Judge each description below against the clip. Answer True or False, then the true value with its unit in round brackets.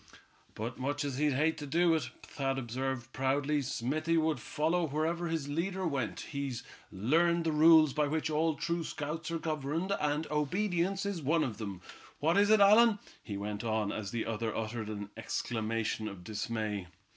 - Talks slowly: False (175 wpm)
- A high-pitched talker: False (145 Hz)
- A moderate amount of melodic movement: False (6.0 semitones)